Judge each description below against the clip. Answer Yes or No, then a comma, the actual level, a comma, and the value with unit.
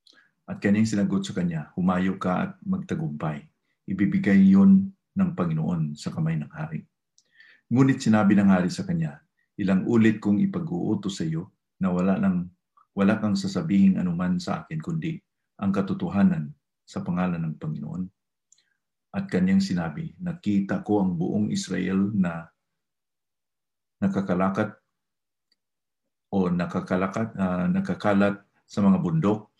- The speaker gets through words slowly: Yes, slow, 125 wpm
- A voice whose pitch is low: Yes, low, 130 Hz